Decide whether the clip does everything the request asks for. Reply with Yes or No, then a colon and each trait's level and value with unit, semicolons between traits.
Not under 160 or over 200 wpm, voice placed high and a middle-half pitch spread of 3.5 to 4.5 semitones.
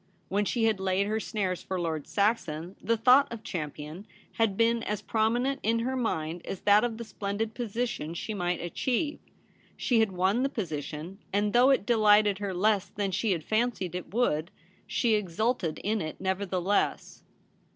Yes: average, 170 wpm; high, 205 Hz; average, 3.9 semitones